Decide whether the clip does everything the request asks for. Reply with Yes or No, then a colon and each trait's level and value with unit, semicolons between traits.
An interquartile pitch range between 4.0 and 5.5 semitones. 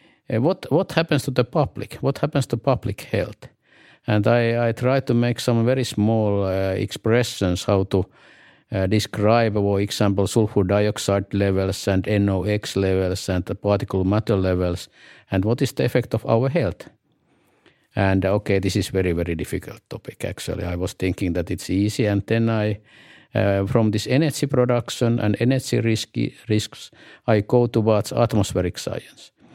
No: average, 3.6 semitones